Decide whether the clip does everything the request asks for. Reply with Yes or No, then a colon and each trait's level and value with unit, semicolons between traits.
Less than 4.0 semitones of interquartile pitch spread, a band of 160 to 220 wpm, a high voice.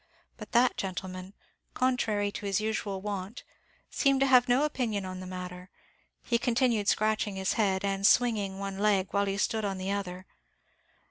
Yes: average, 3.1 semitones; average, 170 wpm; high, 200 Hz